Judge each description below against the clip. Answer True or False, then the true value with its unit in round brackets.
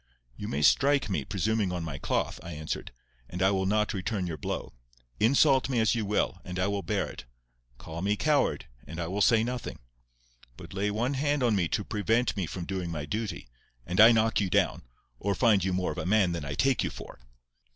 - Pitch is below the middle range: True (100 Hz)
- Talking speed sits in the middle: False (215 wpm)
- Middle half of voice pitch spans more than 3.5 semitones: True (4.1 semitones)